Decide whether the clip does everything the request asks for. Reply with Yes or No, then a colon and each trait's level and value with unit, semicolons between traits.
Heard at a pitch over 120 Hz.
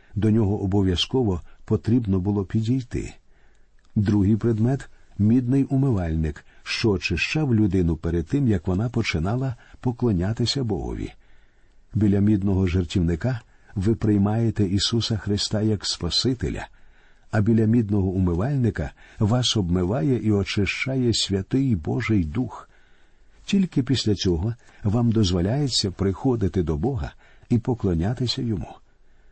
No: low, 110 Hz